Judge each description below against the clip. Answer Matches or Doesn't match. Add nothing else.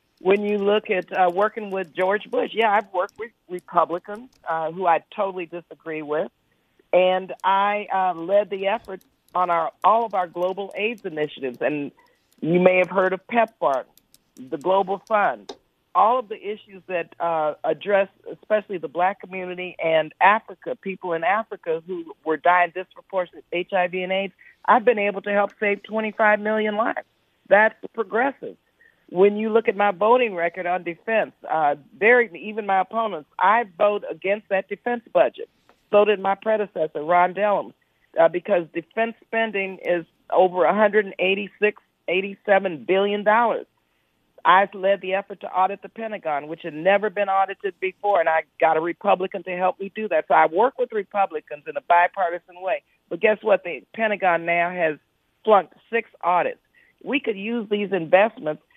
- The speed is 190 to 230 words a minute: Doesn't match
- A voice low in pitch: Doesn't match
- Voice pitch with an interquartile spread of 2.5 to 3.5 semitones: Matches